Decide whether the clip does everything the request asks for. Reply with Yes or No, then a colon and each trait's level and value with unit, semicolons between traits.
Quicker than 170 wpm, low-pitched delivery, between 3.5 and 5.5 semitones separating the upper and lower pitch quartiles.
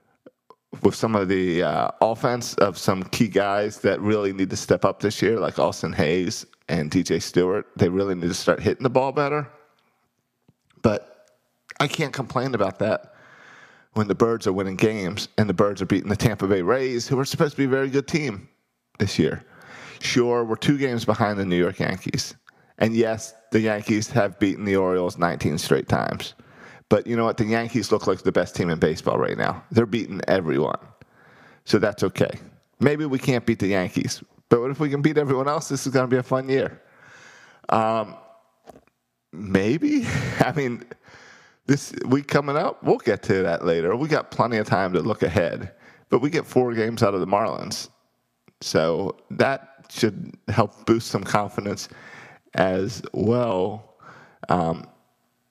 Yes: average, 180 wpm; low, 115 Hz; average, 4.8 semitones